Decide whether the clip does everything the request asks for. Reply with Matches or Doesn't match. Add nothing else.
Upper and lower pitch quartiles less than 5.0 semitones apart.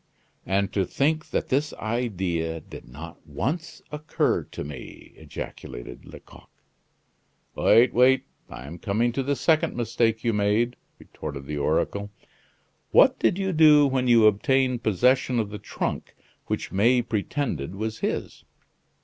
Doesn't match